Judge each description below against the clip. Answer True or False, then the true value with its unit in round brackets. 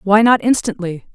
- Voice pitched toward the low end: False (205 Hz)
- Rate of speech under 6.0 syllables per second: True (5.0 syllables/s)